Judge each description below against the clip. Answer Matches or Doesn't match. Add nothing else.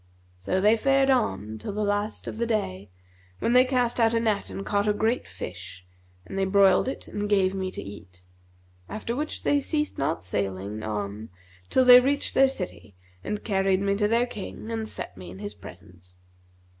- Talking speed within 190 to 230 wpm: Matches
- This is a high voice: Matches